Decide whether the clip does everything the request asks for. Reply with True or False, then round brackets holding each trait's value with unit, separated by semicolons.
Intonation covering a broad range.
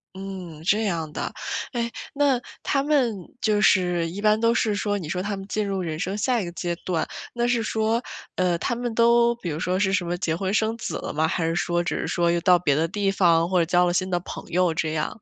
False (4.1 semitones)